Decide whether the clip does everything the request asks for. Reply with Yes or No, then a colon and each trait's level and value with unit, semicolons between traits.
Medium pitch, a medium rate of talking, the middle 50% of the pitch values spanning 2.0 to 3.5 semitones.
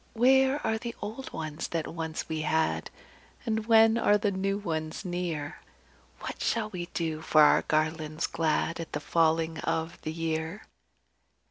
No: medium, 165 Hz; average, 155 wpm; average, 5.2 semitones